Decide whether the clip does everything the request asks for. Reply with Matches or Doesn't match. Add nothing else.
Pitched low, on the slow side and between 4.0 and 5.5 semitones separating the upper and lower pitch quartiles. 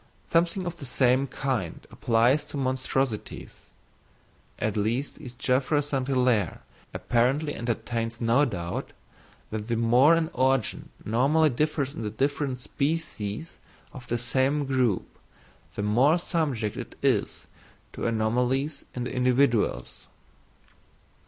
Doesn't match